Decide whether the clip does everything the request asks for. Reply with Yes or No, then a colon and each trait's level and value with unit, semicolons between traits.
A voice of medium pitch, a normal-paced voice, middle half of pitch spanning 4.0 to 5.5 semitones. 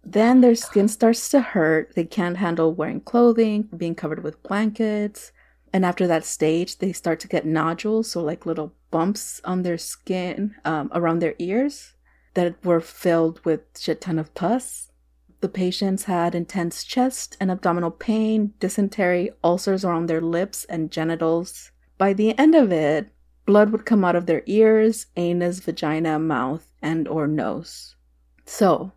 Yes: medium, 175 Hz; average, 160 wpm; average, 4.3 semitones